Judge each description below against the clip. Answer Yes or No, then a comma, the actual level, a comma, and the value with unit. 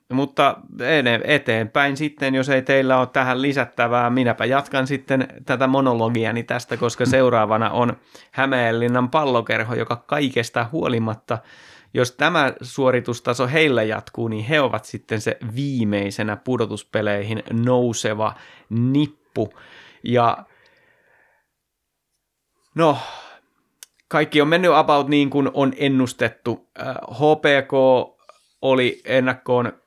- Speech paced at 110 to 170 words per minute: No, average, 100 wpm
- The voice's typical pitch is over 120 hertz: Yes, low, 130 Hz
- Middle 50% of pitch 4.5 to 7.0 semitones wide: No, average, 3.1 semitones